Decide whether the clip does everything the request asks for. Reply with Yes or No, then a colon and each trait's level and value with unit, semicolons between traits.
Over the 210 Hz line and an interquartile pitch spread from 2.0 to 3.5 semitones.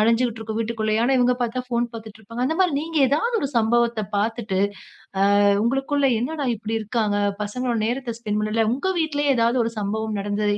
Yes: high, 230 Hz; average, 2.9 semitones